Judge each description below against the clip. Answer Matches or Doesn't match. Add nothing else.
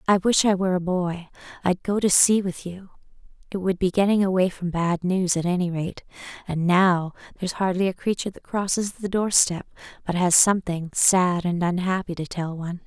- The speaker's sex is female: Matches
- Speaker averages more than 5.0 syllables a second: Matches